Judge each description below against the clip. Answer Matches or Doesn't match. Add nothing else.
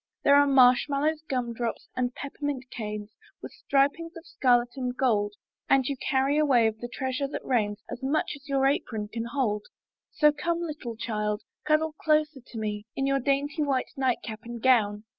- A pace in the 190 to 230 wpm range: Doesn't match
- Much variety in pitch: Doesn't match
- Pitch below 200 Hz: Doesn't match